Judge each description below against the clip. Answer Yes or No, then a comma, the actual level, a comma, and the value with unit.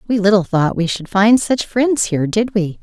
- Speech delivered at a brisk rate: Yes, fast, 235 wpm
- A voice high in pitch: Yes, high, 205 Hz